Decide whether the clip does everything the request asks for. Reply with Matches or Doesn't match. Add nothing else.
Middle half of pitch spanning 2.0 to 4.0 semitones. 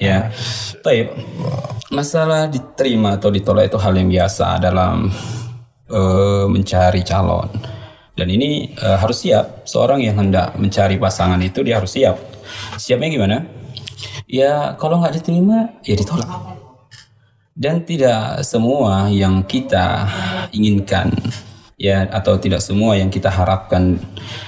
Doesn't match